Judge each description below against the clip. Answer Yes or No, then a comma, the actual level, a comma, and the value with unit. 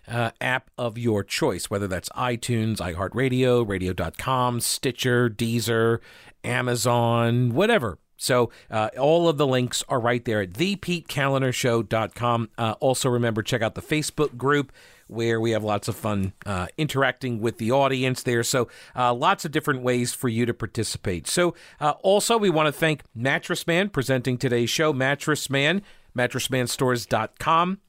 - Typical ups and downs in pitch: Yes, average, 3.5 semitones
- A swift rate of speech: No, average, 145 wpm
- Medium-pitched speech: No, low, 125 Hz